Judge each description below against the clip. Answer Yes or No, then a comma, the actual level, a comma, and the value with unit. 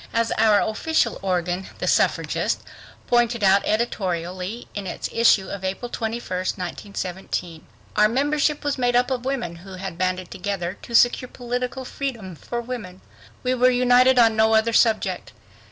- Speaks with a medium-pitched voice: No, high, 220 Hz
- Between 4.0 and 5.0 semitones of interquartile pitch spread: Yes, average, 4.7 semitones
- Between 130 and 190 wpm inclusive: Yes, average, 155 wpm